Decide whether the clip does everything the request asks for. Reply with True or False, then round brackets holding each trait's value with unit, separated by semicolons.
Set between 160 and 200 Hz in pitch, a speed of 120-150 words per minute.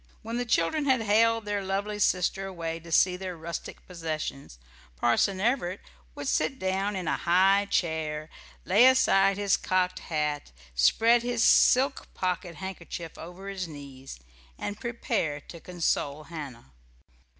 True (185 Hz; 140 wpm)